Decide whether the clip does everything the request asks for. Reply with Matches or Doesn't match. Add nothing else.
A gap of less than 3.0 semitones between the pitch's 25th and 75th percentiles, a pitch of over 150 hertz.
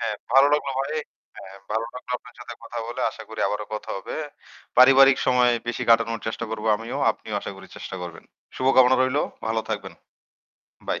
Doesn't match